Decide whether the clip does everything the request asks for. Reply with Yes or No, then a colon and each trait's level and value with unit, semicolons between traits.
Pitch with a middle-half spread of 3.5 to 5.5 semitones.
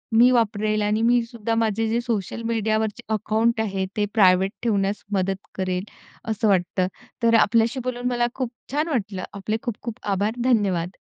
No: average, 2.9 semitones